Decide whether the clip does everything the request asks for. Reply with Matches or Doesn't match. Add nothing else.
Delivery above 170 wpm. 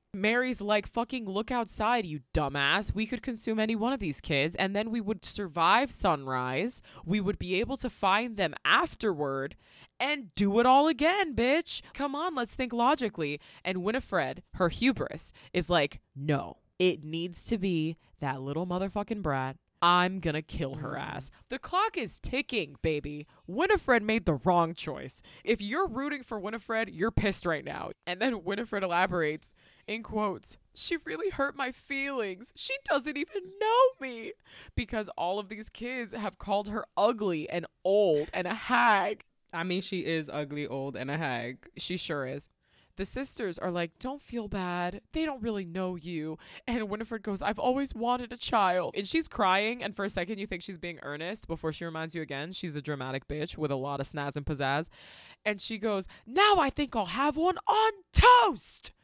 Matches